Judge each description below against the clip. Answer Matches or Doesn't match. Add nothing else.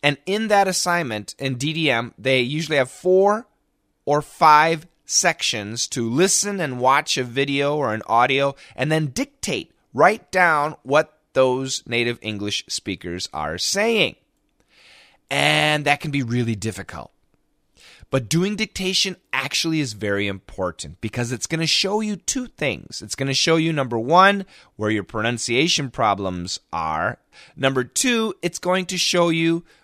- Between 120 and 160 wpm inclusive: Matches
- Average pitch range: Doesn't match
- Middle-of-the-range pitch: Matches